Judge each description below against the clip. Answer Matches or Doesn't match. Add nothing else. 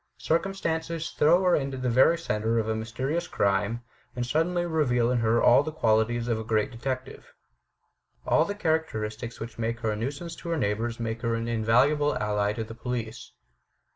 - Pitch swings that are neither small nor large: Doesn't match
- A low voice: Matches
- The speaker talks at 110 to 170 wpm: Doesn't match